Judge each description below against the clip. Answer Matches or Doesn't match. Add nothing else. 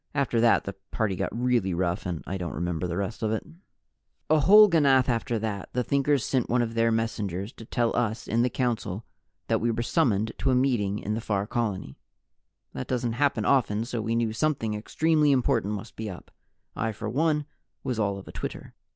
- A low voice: Matches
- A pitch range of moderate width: Matches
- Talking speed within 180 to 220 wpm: Matches